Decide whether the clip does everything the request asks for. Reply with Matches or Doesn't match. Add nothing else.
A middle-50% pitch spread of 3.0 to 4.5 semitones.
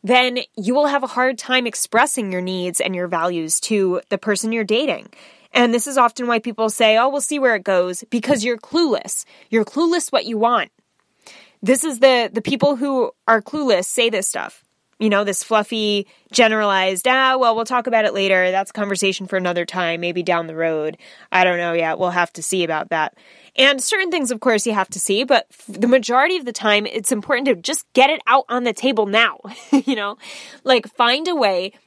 Doesn't match